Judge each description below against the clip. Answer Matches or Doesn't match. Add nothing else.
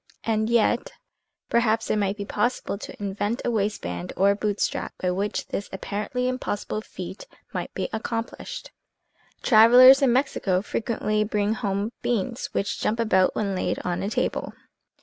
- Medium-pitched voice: Doesn't match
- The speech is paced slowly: Doesn't match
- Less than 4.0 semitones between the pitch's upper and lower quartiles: Matches